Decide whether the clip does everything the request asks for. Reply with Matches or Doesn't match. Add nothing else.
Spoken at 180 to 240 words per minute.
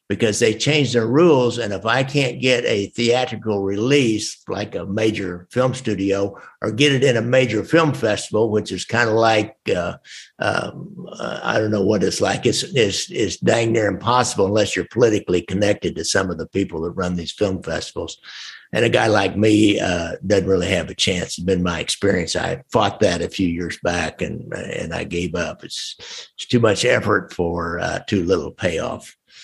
Matches